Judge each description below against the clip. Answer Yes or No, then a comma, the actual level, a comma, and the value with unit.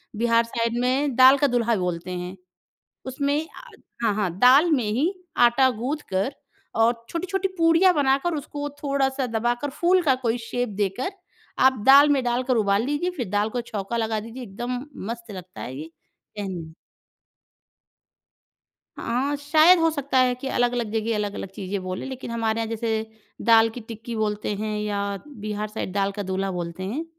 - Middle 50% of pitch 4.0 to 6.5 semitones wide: Yes, average, 4.6 semitones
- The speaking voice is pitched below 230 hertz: No, high, 235 Hz